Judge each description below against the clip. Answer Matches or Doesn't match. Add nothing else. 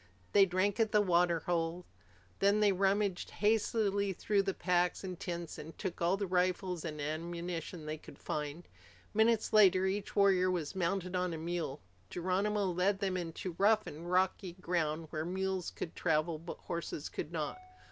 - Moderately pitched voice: Matches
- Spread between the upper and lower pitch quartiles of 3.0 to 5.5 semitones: Doesn't match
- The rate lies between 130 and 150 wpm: Doesn't match